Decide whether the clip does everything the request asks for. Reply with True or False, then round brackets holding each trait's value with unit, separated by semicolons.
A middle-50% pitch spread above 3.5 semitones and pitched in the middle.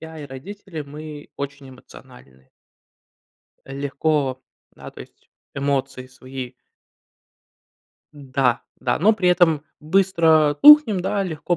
True (4.5 semitones; 145 Hz)